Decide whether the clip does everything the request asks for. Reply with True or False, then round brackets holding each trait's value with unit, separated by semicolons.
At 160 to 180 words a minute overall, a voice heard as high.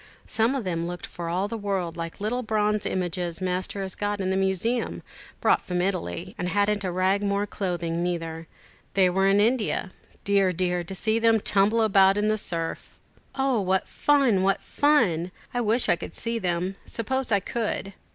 False (190 wpm; 195 Hz)